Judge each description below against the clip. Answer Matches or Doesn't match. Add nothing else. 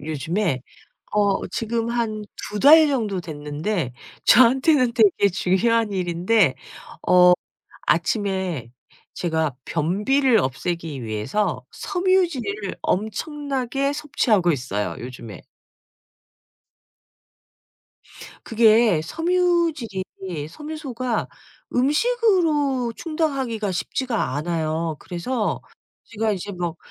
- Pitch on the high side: Matches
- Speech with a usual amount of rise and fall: Doesn't match